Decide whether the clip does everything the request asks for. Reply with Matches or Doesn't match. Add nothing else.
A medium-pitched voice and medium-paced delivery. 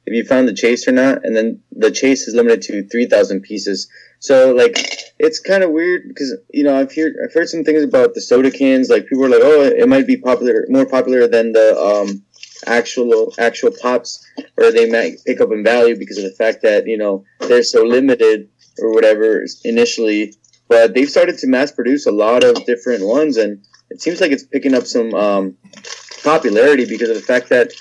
Doesn't match